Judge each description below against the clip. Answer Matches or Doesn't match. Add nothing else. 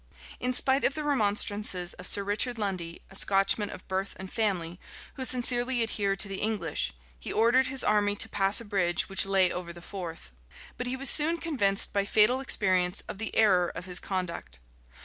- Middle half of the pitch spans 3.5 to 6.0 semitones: Matches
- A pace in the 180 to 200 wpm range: Matches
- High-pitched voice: Matches